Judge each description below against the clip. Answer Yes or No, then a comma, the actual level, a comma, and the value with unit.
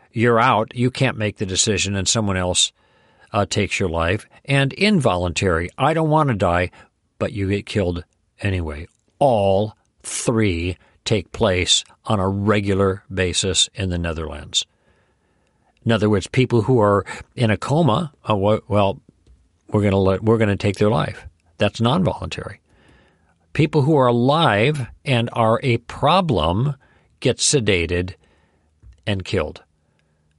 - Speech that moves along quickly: No, average, 140 wpm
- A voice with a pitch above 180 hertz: No, low, 100 Hz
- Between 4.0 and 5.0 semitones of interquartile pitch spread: Yes, average, 4.3 semitones